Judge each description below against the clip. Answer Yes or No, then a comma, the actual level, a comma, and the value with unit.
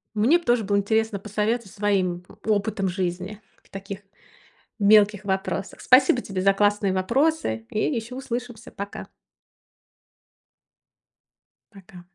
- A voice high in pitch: Yes, high, 205 Hz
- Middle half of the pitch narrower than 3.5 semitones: Yes, narrow, 2.4 semitones